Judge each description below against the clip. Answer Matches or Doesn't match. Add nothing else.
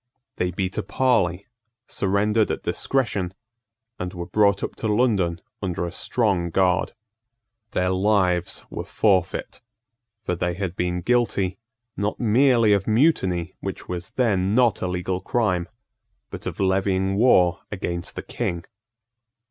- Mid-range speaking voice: Doesn't match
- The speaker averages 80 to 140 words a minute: Matches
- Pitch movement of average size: Matches